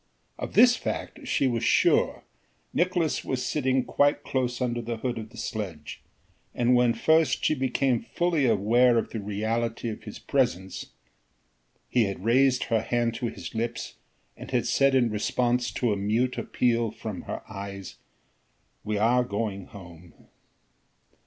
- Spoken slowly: No, average, 150 wpm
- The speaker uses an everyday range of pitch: Yes, average, 3.1 semitones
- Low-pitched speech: Yes, low, 120 Hz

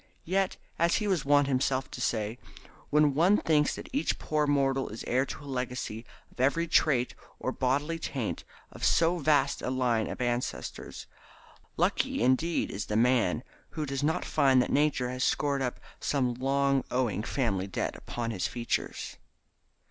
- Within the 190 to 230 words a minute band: No, average, 170 wpm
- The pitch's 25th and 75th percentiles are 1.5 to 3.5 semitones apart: Yes, average, 3.1 semitones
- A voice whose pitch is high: No, low, 135 Hz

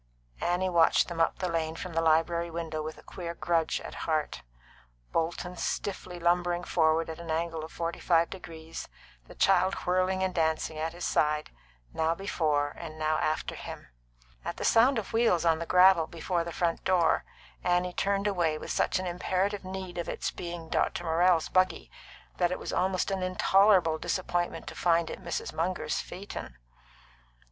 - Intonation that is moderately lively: No, narrow, 2.1 semitones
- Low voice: No, medium, 170 Hz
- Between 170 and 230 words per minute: Yes, average, 175 wpm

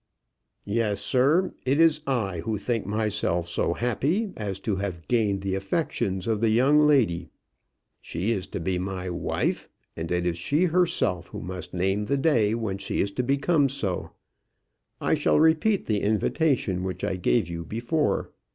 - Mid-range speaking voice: No, low, 105 Hz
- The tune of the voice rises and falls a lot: Yes, wide, 6.7 semitones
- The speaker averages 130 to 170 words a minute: Yes, average, 160 wpm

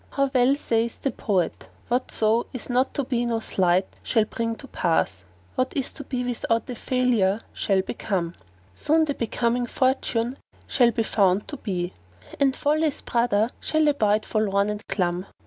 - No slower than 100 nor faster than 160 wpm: No, average, 170 wpm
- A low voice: No, high, 230 Hz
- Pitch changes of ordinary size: Yes, average, 4.3 semitones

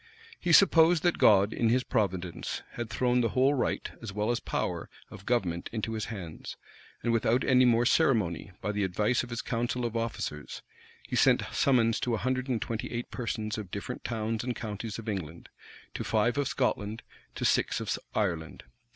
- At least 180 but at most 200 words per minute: Yes, average, 185 wpm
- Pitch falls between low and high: No, low, 115 Hz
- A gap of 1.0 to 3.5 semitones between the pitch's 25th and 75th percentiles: Yes, average, 3.1 semitones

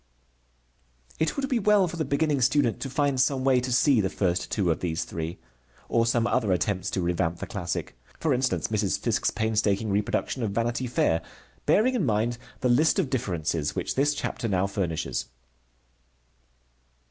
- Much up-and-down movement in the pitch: Yes, wide, 6.1 semitones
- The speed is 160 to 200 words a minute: Yes, average, 170 wpm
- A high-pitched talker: No, low, 115 Hz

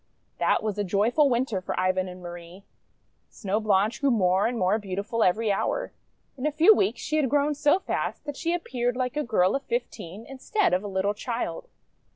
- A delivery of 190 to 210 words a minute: Yes, average, 200 wpm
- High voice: Yes, high, 225 Hz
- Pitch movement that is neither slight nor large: No, wide, 6.7 semitones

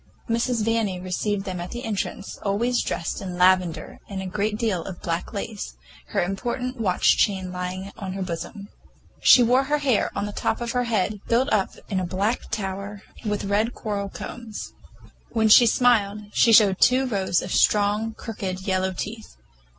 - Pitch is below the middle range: No, high, 205 Hz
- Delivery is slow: No, average, 175 wpm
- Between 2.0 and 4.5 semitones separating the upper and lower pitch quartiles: Yes, average, 3.3 semitones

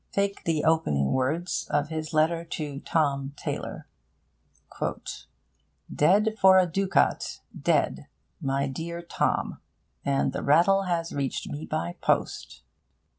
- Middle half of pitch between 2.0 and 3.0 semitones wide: No, average, 3.7 semitones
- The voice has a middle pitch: Yes, medium, 160 Hz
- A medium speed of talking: No, slow, 120 wpm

